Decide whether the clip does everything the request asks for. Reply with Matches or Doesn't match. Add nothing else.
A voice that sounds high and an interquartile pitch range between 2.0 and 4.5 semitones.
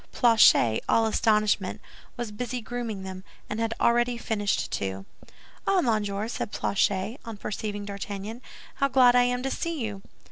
Matches